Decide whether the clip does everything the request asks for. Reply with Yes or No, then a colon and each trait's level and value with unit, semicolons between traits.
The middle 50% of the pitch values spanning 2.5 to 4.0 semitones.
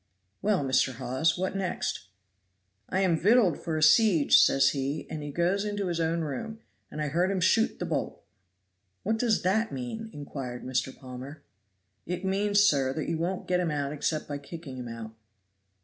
No: wide, 5.5 semitones